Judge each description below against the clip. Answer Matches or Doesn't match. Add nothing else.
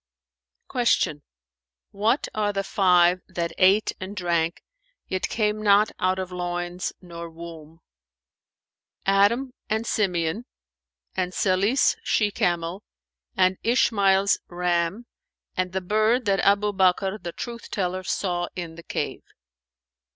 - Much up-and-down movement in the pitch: Doesn't match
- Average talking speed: Doesn't match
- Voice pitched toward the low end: Doesn't match